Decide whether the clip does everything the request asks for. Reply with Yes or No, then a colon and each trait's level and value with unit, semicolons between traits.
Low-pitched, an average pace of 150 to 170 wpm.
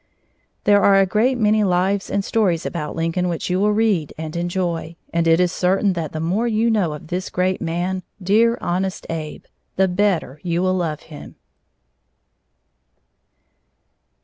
No: medium, 180 Hz; average, 160 wpm